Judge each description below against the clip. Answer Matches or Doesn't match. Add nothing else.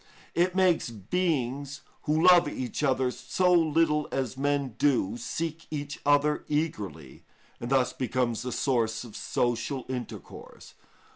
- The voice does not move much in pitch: Doesn't match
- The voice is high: Doesn't match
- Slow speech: Matches